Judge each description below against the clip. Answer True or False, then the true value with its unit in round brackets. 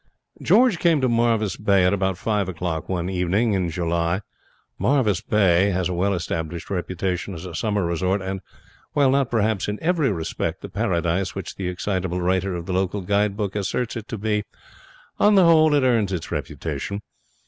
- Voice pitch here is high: False (95 Hz)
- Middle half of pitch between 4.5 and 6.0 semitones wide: False (3.5 semitones)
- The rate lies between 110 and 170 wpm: False (180 wpm)